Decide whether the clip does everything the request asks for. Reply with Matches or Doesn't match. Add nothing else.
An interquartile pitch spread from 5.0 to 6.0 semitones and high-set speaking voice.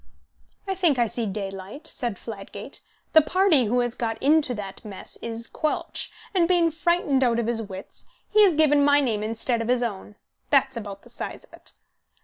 Matches